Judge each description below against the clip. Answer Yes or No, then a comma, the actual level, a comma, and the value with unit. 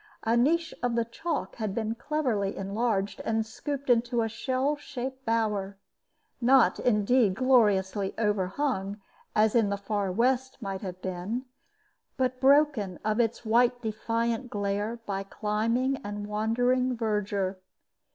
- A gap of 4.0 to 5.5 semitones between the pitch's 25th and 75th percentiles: No, average, 3.6 semitones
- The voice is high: Yes, high, 225 Hz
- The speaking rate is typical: No, slow, 130 wpm